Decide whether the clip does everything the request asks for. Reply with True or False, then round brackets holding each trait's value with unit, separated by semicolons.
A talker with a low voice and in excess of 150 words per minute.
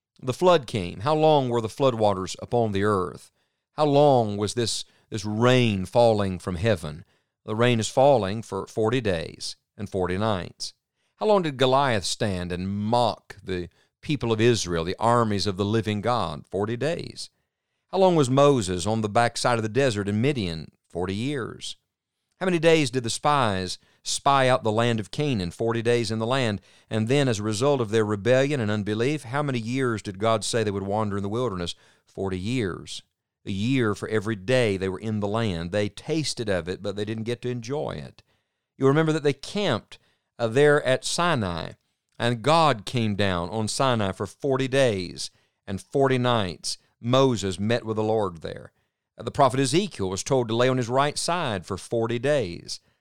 True (115 Hz; 190 wpm)